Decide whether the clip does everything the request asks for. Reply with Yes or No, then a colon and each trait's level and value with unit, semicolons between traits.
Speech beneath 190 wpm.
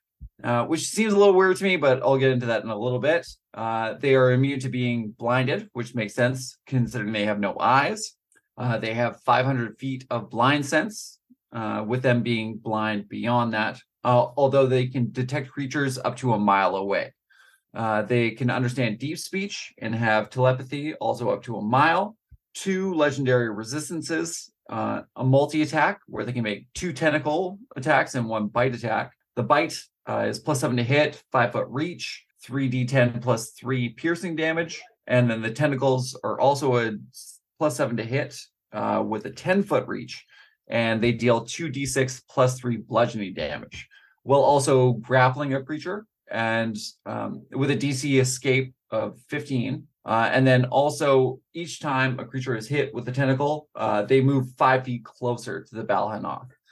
Yes: average, 175 wpm